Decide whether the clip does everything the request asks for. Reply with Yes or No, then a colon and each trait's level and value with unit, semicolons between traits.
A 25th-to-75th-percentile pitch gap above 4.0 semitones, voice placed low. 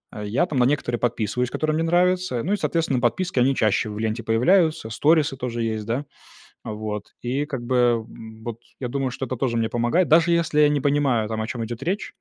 Yes: average, 5.1 semitones; low, 125 Hz